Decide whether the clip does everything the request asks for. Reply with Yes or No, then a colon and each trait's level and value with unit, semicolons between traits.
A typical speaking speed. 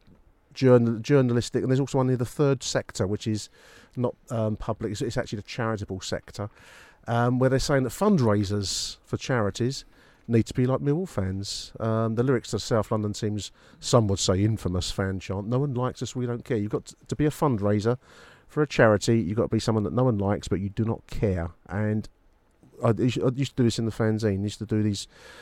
No: fast, 220 wpm